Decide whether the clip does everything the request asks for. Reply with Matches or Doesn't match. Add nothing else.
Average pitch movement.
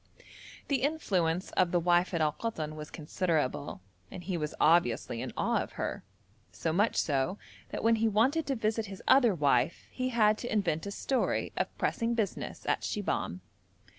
Doesn't match